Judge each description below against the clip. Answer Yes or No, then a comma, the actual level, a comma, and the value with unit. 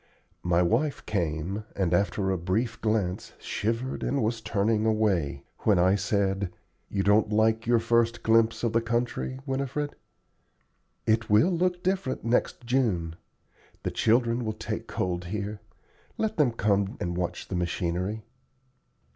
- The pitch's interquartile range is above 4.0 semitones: No, average, 3.7 semitones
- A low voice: Yes, low, 110 Hz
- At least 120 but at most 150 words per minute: Yes, average, 140 wpm